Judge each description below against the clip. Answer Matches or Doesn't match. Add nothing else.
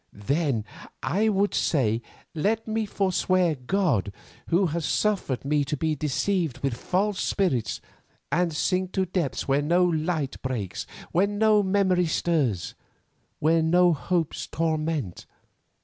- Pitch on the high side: Doesn't match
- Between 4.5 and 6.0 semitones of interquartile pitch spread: Matches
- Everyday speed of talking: Doesn't match